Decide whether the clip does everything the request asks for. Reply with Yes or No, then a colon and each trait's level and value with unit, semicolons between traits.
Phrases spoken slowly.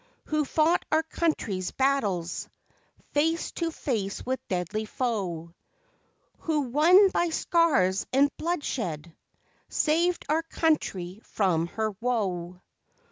Yes: slow, 105 wpm